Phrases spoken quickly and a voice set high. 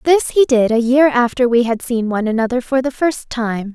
Yes: fast, 240 wpm; high, 245 Hz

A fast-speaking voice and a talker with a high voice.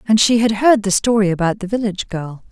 Yes: fast, 240 wpm; high, 205 Hz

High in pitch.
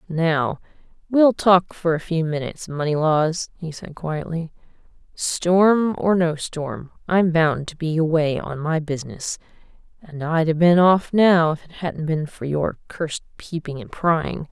No: medium, 165 Hz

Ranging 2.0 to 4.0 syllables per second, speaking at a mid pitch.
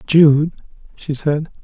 Yes: 3.1 syllables/s; medium, 150 Hz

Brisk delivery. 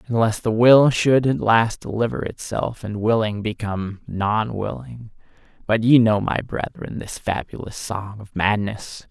No: average, 150 wpm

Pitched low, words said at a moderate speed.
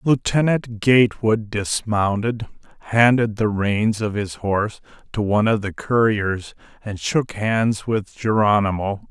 No: low, 110 Hz; slow, 125 wpm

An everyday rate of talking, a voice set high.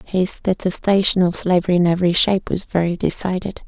No: average, 165 wpm; medium, 180 Hz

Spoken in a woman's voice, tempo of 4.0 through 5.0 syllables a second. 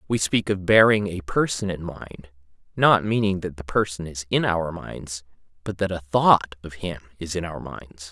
No: male; 4.5 syllables/s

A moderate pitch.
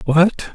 Yes: medium, 170 Hz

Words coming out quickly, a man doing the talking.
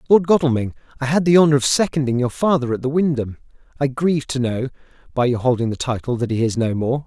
Yes: fast, 230 wpm; male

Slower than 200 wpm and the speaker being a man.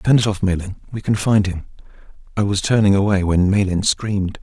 No: fast, 205 wpm; male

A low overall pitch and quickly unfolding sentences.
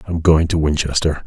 No: very low, 80 Hz; average, 190 wpm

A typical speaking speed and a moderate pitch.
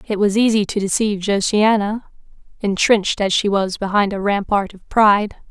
No: average, 165 wpm; high, 205 Hz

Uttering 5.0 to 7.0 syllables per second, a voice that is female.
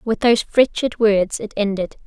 Yes: 5.2 syllables/s; female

